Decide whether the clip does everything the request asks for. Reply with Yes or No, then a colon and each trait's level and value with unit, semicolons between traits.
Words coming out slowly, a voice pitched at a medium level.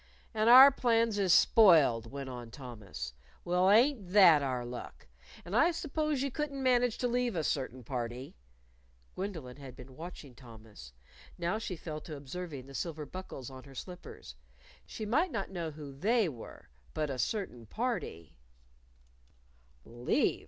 No: average, 155 wpm; medium, 160 Hz